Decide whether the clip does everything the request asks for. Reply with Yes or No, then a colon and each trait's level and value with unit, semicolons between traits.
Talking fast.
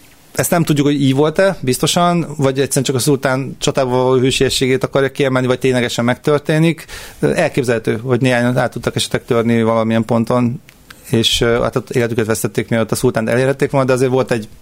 Yes: fast, 170 wpm